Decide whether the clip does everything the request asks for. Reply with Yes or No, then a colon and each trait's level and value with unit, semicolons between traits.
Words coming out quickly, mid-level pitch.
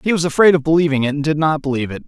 Yes: fast, 315 wpm; medium, 150 Hz